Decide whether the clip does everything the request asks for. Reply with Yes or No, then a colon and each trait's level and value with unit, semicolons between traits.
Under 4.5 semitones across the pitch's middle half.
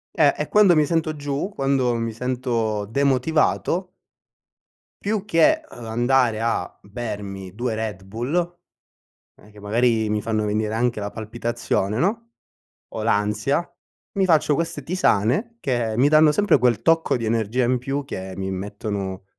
No: wide, 5.7 semitones